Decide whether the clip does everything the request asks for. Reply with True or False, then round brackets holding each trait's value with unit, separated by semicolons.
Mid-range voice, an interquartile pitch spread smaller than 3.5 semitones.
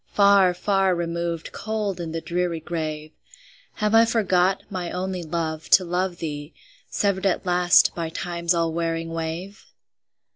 True (175 Hz; 2.5 semitones)